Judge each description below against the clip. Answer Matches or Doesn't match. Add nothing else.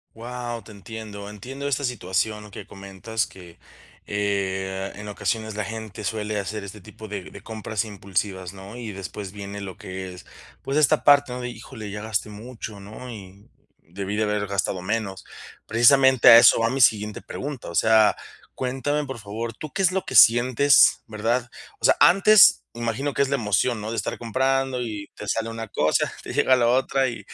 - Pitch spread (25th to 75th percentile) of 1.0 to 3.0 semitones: Doesn't match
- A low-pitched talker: Matches